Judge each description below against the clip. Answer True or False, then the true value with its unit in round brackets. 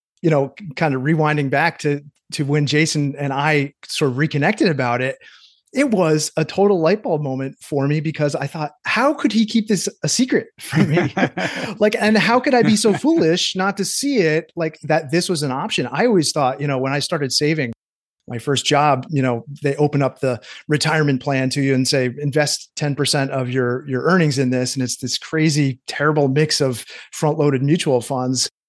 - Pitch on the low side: False (150 Hz)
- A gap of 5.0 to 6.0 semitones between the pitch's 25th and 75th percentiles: False (3.4 semitones)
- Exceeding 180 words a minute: True (205 wpm)